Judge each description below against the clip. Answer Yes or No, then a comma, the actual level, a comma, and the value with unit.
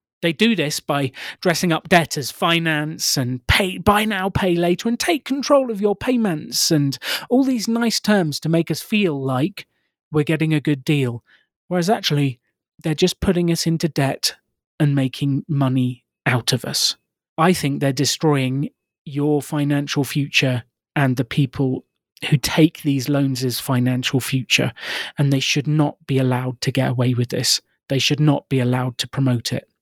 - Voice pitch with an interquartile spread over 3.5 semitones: Yes, average, 4.3 semitones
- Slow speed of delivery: No, average, 175 wpm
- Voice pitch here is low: No, medium, 150 Hz